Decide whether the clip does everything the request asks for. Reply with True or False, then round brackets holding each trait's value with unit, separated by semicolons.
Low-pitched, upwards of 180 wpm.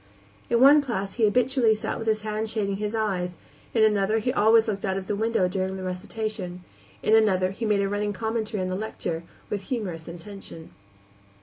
False (210 Hz; 195 wpm)